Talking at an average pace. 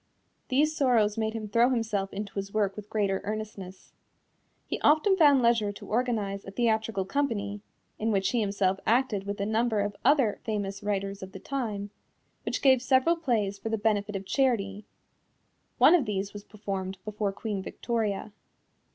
Yes: average, 170 wpm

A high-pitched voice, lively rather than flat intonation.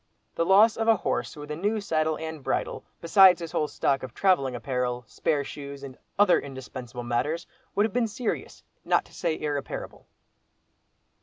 No: medium, 155 Hz; wide, 6.1 semitones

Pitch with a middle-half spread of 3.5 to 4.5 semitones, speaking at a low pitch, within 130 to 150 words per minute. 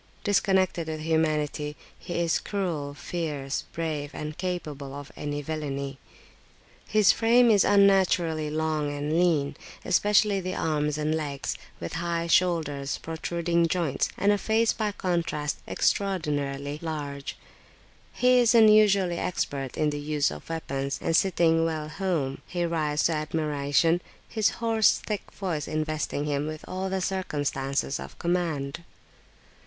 No: average, 3.9 semitones; medium, 160 Hz; slow, 135 wpm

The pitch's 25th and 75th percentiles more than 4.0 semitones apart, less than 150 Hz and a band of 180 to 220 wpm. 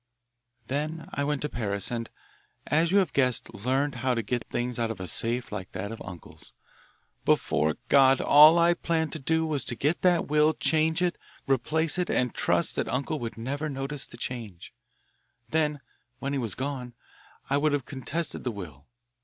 Yes: average, 4.7 semitones; low, 135 Hz; average, 185 wpm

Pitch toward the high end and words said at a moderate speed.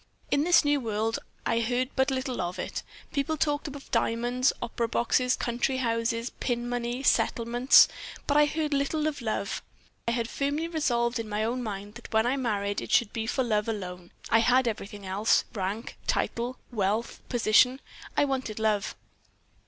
Yes: high, 235 Hz; average, 170 wpm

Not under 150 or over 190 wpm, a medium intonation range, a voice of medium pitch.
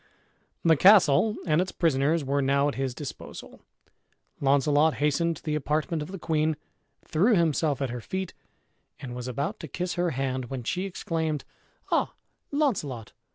Yes: average, 155 wpm; average, 3.7 semitones; medium, 150 Hz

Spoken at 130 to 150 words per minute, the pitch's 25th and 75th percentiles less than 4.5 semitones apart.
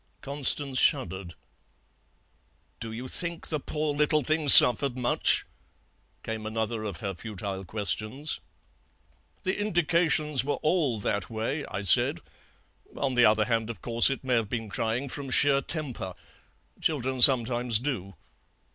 No: slow, 135 wpm; average, 4.8 semitones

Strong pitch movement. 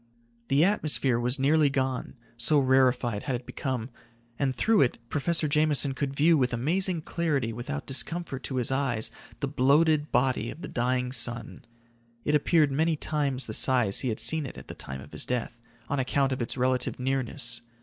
No: average, 3.1 semitones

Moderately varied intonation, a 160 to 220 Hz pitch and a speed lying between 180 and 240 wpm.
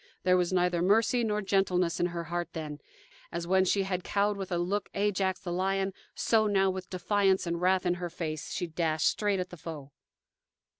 No: narrow, 2.0 semitones; medium, 185 Hz; average, 200 wpm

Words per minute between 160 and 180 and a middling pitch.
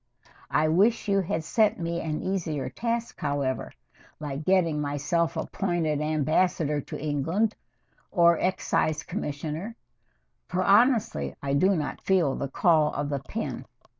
No: slow, 135 wpm; medium, 160 Hz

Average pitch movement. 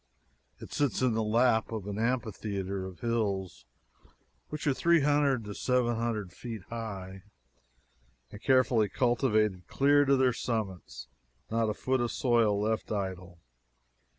Yes: average, 3.9 semitones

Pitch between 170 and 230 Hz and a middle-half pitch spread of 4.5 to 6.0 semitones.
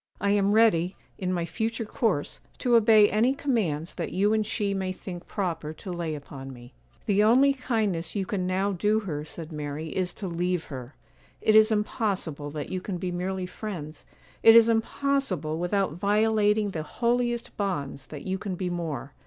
Yes: high, 190 Hz; average, 4.8 semitones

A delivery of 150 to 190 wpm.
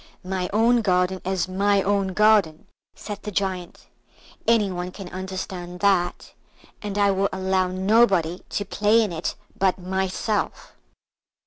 No: slow, 135 wpm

